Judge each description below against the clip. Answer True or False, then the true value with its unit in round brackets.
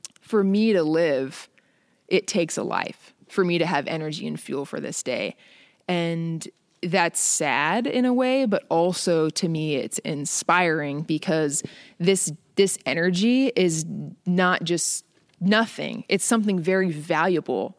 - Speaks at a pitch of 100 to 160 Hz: False (180 Hz)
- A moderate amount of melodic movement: True (3.5 semitones)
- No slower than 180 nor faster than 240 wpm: False (140 wpm)